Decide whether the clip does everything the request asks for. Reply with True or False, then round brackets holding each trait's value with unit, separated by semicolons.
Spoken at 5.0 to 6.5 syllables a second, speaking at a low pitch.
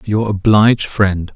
False (4.0 syllables/s; 105 Hz)